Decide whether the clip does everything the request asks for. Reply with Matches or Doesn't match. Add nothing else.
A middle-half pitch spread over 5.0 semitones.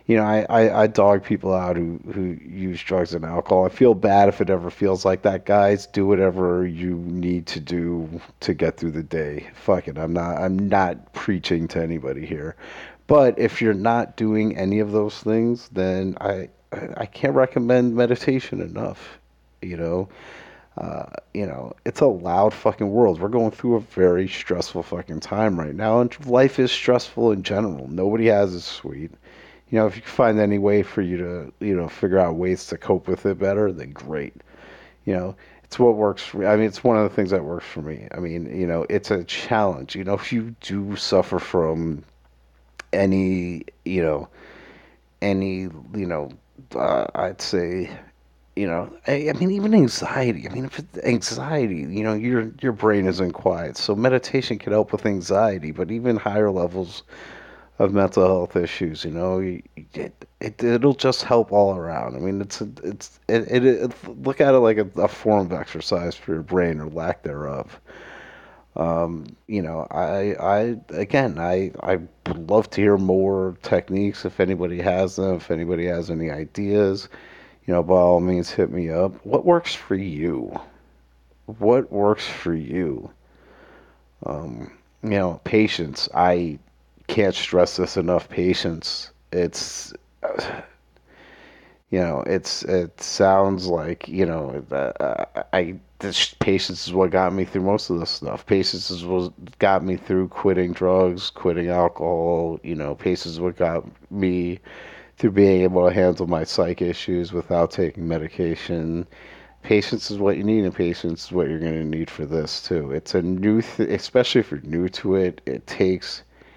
Doesn't match